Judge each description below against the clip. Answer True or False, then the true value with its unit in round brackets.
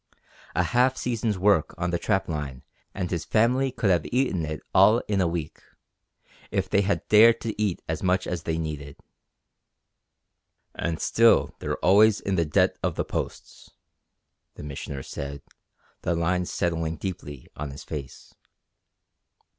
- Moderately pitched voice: False (90 Hz)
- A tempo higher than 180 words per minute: False (155 wpm)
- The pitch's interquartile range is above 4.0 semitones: True (5.2 semitones)